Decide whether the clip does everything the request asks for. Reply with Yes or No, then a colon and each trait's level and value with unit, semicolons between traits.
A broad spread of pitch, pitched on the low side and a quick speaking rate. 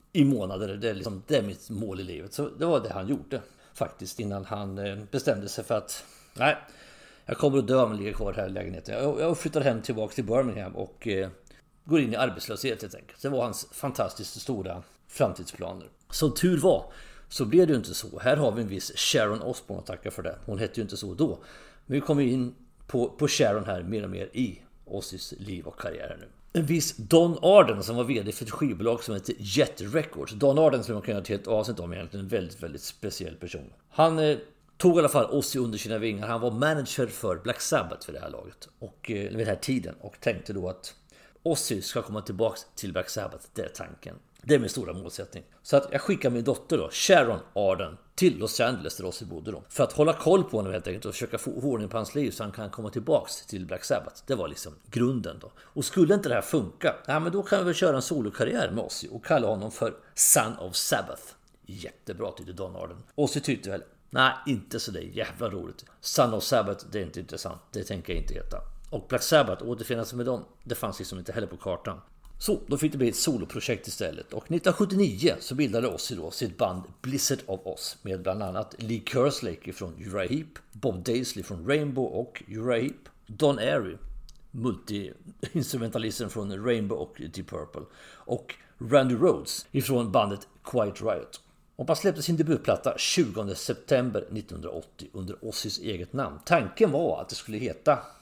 Yes: wide, 5.7 semitones; low, 115 Hz; fast, 210 wpm